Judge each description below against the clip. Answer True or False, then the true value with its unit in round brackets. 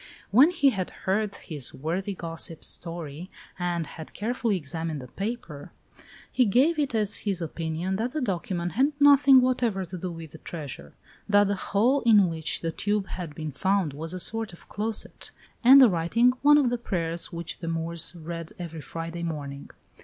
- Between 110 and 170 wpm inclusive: False (180 wpm)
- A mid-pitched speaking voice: True (180 Hz)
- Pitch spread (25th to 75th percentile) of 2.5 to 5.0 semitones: False (5.4 semitones)